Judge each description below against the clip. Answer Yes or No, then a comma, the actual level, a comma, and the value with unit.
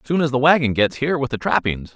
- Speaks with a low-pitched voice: Yes, low, 130 Hz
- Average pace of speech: No, fast, 275 wpm